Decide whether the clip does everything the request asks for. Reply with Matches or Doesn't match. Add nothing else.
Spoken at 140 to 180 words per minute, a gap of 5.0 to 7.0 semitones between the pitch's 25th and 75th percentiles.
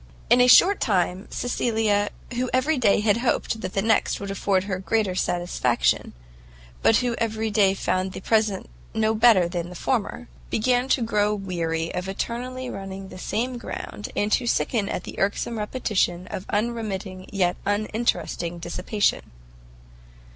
Doesn't match